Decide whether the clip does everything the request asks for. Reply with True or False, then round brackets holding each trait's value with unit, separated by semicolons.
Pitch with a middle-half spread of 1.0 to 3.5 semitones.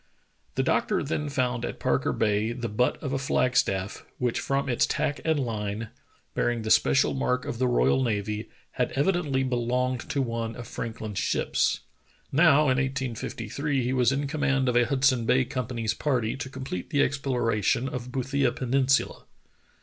True (2.7 semitones)